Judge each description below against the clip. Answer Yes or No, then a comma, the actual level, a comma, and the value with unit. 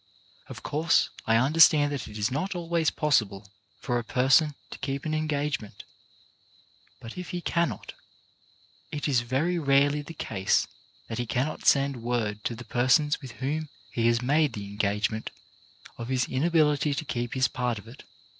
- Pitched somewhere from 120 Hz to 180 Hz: Yes, low, 135 Hz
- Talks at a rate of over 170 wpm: No, average, 165 wpm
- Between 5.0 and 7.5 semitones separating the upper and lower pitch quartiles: No, average, 4.4 semitones